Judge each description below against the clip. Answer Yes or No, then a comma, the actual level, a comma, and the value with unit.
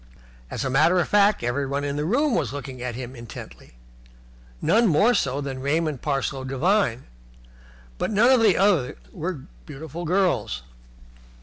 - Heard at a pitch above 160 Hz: No, medium, 145 Hz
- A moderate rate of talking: Yes, average, 150 wpm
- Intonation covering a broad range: Yes, wide, 6.3 semitones